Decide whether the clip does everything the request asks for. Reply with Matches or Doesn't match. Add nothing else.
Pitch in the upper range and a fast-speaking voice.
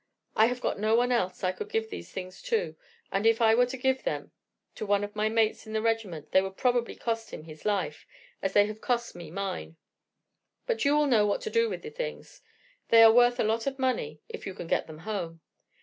Matches